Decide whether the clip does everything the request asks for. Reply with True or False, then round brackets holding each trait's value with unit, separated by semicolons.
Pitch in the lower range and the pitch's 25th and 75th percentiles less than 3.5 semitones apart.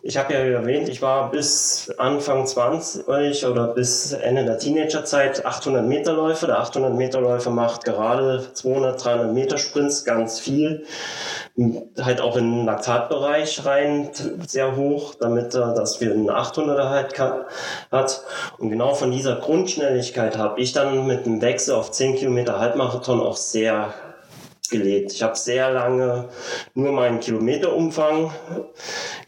True (130 Hz; 3.1 semitones)